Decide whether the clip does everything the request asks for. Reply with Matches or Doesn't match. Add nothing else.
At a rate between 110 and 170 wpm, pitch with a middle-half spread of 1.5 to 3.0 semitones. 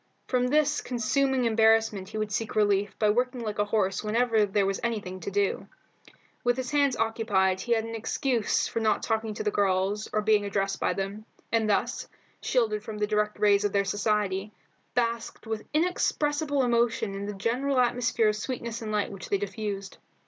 Doesn't match